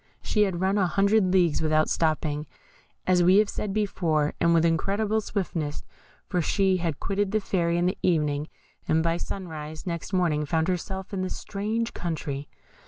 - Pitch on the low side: No, medium, 175 Hz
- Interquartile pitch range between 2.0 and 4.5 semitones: Yes, average, 3.6 semitones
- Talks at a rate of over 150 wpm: Yes, average, 170 wpm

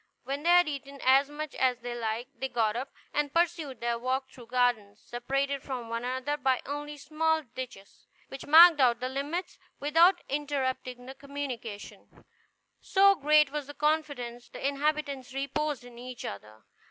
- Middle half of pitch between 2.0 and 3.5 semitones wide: Yes, average, 3.2 semitones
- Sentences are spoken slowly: No, average, 165 wpm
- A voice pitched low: No, very high, 275 Hz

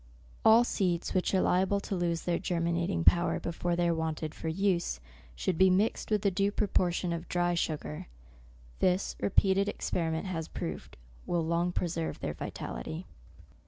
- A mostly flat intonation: Yes, narrow, 2.3 semitones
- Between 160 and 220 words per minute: Yes, average, 165 wpm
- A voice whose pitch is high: No, medium, 175 Hz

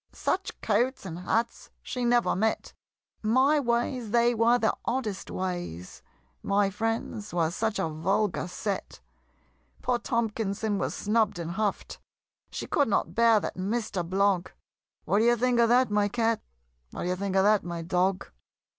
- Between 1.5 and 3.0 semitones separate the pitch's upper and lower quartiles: No, average, 3.7 semitones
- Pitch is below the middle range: No, high, 215 Hz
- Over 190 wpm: No, average, 155 wpm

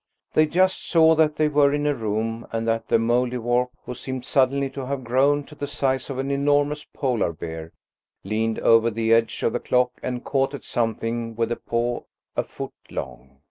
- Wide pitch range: No, average, 3.8 semitones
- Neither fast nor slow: Yes, average, 195 wpm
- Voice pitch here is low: Yes, low, 125 Hz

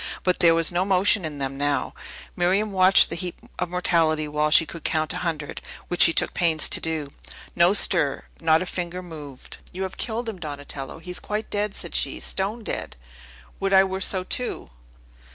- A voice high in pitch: No, medium, 175 Hz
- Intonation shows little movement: No, average, 3.4 semitones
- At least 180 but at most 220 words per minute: Yes, average, 195 wpm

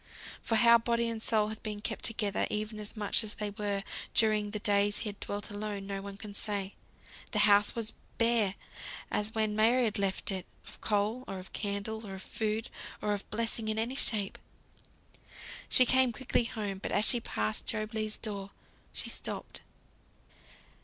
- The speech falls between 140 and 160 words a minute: No, average, 180 wpm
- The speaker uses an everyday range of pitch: No, narrow, 1.7 semitones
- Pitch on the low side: No, high, 210 Hz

